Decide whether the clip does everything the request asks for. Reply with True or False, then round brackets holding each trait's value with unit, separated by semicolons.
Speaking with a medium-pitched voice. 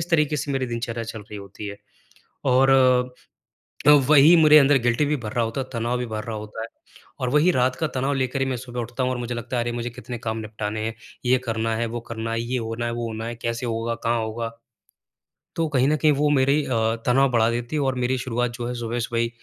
False (120 Hz)